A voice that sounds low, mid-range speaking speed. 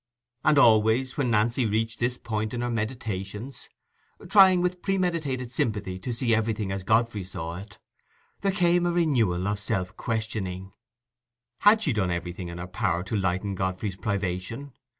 Yes: low, 110 Hz; average, 150 wpm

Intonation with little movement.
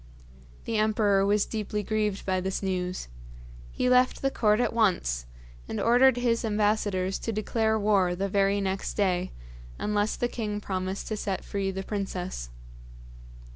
Yes: narrow, 2.3 semitones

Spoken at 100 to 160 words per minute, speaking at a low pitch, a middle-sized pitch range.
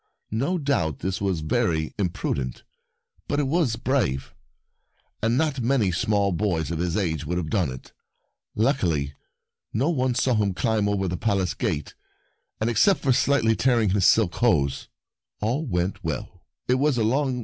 No: average, 150 wpm; low, 100 Hz; wide, 6.5 semitones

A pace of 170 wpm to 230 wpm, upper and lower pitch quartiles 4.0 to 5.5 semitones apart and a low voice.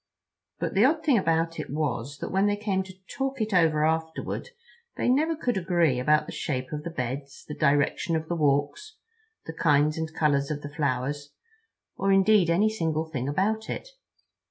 No: average, 185 wpm; average, 5.1 semitones; medium, 160 Hz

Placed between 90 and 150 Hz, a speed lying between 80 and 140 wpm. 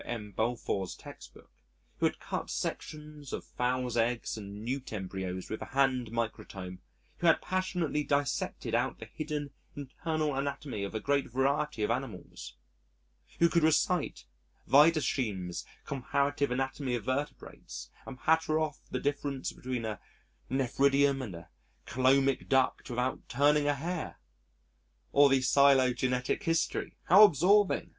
Yes: low, 135 Hz; slow, 135 wpm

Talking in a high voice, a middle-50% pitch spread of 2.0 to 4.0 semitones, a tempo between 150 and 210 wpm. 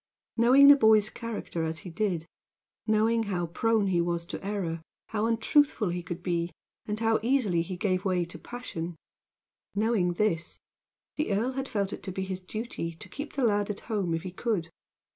No: high, 205 Hz; average, 4.5 semitones; average, 185 wpm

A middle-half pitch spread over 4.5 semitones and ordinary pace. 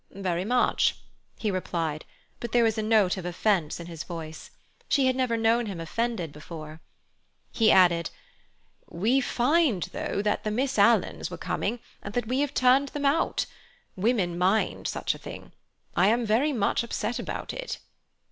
Yes: wide, 5.6 semitones; average, 165 wpm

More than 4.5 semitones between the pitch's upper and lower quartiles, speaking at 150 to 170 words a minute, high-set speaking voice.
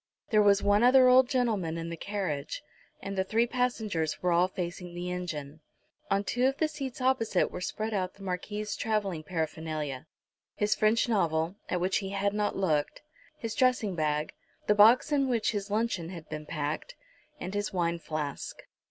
No: average, 4.9 semitones; average, 180 wpm; high, 195 Hz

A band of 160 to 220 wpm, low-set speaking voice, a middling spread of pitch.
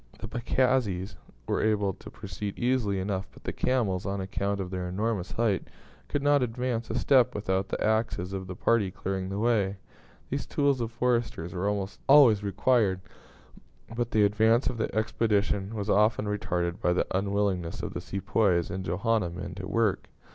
Yes: average, 175 wpm; low, 105 Hz; average, 3.3 semitones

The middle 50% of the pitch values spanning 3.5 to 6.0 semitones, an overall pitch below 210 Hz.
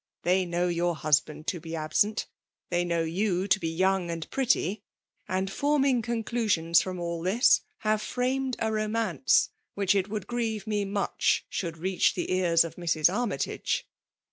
Yes: average, 4.2 semitones; high, 190 Hz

